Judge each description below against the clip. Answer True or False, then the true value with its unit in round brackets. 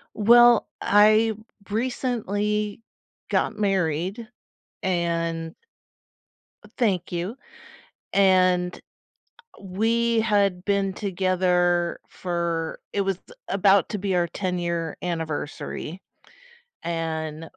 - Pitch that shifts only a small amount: False (3.3 semitones)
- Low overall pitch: False (185 Hz)